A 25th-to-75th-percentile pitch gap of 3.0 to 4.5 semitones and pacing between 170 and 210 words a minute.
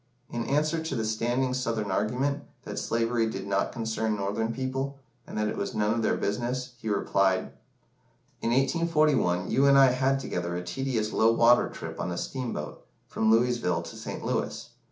Yes: average, 3.7 semitones; average, 175 wpm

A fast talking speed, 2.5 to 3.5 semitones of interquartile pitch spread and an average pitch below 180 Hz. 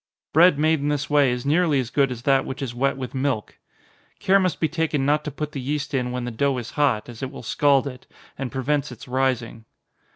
Yes: fast, 235 wpm; average, 2.8 semitones; low, 135 Hz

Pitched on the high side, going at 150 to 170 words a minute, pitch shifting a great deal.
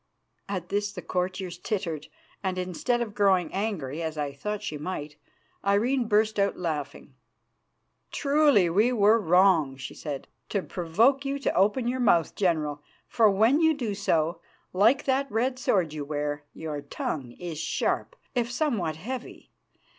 Yes: high, 195 Hz; average, 155 wpm; wide, 6.3 semitones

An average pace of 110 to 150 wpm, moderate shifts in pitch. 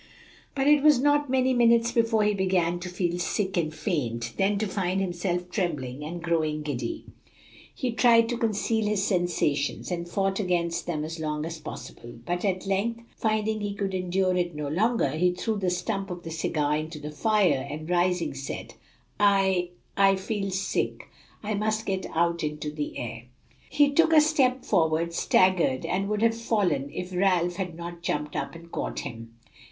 No: average, 180 wpm; average, 4.5 semitones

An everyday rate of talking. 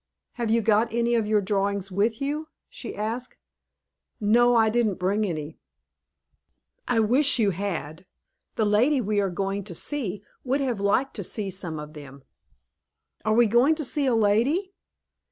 Yes: average, 165 wpm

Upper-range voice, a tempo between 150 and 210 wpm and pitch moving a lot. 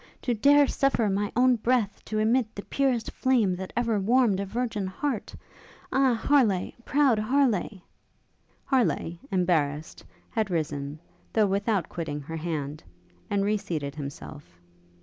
No: high, 205 Hz; average, 140 wpm; wide, 6.1 semitones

